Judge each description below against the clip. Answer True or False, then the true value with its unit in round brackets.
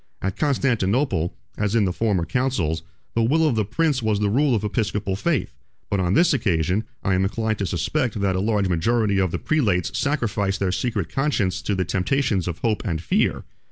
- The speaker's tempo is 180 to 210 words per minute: True (195 wpm)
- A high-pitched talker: False (105 Hz)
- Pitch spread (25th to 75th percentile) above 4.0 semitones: True (4.7 semitones)